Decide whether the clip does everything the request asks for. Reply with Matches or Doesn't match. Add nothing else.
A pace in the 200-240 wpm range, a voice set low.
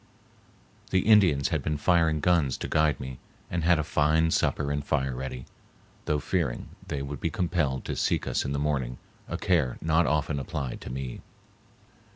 Doesn't match